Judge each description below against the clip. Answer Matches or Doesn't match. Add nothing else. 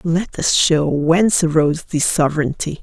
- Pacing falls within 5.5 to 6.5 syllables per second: Doesn't match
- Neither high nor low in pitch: Matches